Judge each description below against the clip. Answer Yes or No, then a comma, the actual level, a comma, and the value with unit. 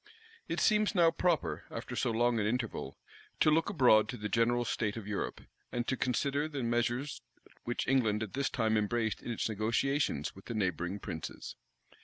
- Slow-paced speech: No, average, 180 wpm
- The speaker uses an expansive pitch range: No, average, 4.1 semitones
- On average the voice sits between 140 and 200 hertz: No, low, 120 Hz